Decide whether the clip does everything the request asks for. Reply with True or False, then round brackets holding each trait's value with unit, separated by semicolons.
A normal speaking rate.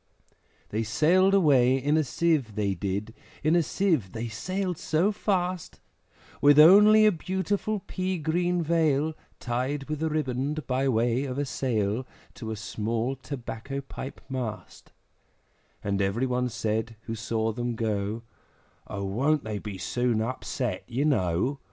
True (145 wpm)